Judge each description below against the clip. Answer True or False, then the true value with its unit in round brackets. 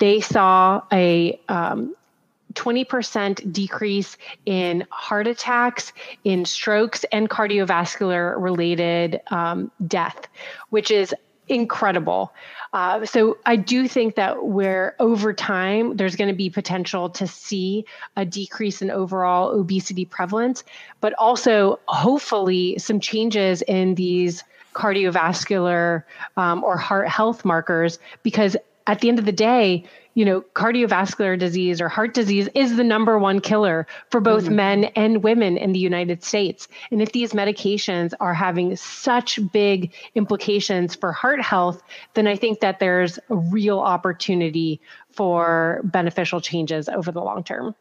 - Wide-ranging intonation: False (3.1 semitones)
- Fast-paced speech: False (135 wpm)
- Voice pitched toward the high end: True (200 Hz)